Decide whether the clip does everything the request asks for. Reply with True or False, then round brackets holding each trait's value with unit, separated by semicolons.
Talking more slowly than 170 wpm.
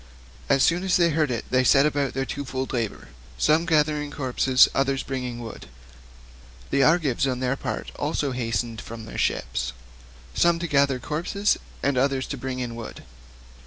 False (195 wpm)